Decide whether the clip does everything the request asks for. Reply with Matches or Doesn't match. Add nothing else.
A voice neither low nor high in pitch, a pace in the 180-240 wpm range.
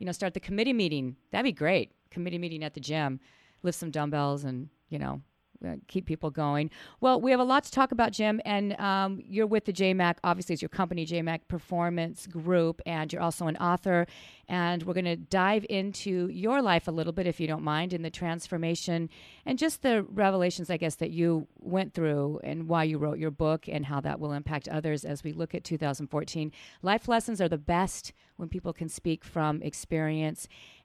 Matches